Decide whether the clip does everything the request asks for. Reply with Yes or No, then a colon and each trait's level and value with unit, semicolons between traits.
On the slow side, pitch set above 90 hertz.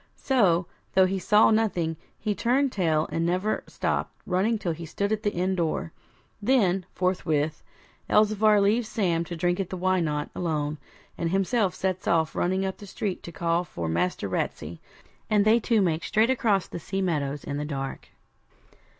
No: average, 175 wpm; medium, 185 Hz